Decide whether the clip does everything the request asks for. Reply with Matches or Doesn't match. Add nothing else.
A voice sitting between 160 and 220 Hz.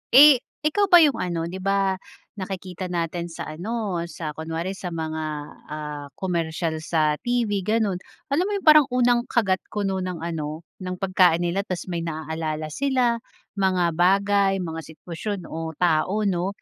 Matches